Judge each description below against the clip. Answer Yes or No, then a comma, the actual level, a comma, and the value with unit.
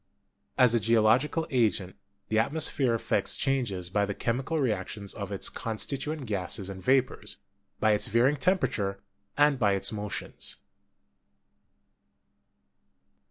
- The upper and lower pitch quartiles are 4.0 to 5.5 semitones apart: Yes, average, 4.9 semitones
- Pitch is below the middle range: Yes, low, 110 Hz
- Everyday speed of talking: No, slow, 120 wpm